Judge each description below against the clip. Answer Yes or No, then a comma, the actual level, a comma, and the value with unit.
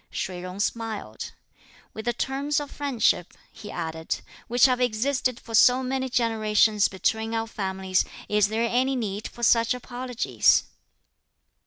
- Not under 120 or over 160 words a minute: Yes, average, 140 wpm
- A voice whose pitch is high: Yes, high, 225 Hz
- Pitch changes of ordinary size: Yes, average, 3.2 semitones